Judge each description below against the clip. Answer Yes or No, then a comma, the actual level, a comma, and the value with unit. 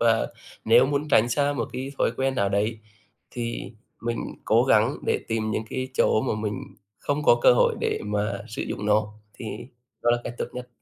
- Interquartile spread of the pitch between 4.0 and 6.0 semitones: No, average, 3.3 semitones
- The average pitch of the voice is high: No, low, 120 Hz